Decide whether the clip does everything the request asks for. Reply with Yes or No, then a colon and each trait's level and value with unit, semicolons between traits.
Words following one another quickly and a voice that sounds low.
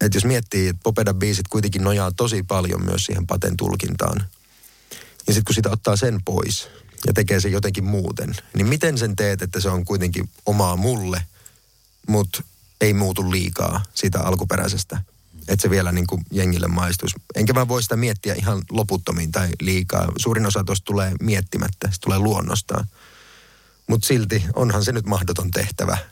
Yes: fast, 165 wpm; low, 100 Hz